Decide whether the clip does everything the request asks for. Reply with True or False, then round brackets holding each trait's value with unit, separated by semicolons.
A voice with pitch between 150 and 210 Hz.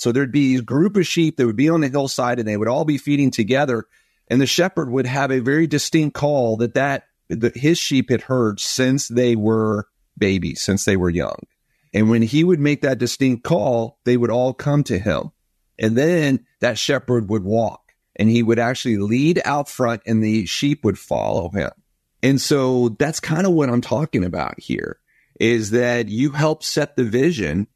False (130 Hz)